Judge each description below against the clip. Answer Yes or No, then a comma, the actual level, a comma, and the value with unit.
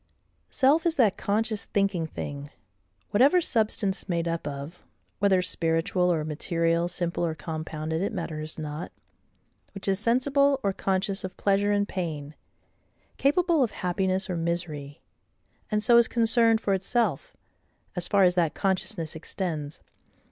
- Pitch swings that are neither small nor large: Yes, average, 4.6 semitones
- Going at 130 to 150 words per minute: Yes, slow, 135 wpm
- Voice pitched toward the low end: No, medium, 185 Hz